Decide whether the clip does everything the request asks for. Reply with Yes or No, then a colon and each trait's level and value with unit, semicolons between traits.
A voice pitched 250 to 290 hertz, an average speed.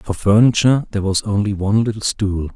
No: low, 105 Hz; average, 190 wpm